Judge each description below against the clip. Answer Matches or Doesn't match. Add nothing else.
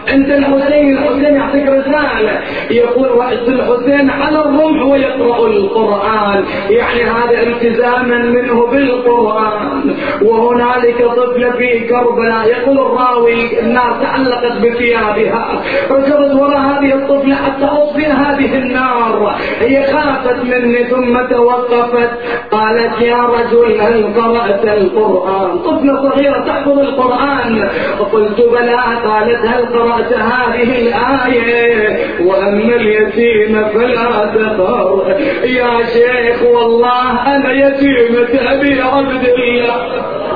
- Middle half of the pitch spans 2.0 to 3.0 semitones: Matches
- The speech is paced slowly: Doesn't match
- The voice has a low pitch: Doesn't match